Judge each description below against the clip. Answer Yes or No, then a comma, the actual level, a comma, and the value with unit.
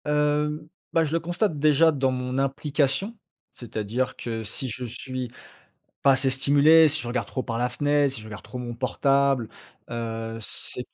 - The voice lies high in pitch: No, low, 135 Hz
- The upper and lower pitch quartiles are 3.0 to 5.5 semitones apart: Yes, average, 3.6 semitones